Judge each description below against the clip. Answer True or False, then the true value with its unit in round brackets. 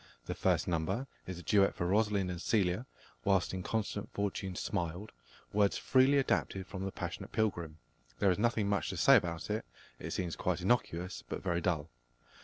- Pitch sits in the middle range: False (95 Hz)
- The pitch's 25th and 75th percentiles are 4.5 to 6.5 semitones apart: False (3.1 semitones)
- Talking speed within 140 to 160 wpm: False (175 wpm)